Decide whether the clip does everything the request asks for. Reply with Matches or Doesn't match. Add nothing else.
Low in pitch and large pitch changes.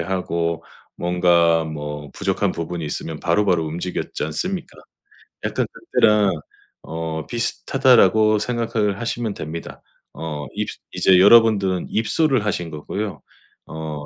Doesn't match